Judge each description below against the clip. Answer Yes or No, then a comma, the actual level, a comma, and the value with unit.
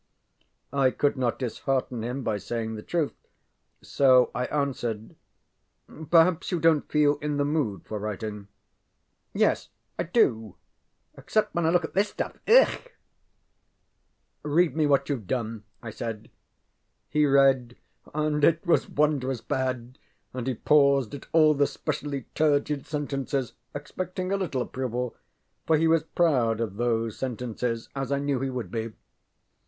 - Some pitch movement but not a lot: Yes, average, 4.3 semitones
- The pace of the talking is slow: No, average, 150 wpm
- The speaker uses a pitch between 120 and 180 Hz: Yes, low, 135 Hz